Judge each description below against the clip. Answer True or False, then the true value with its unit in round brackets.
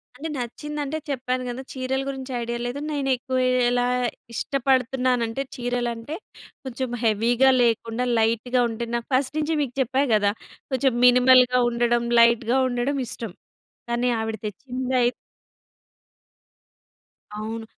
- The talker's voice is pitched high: True (250 Hz)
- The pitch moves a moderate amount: False (2.0 semitones)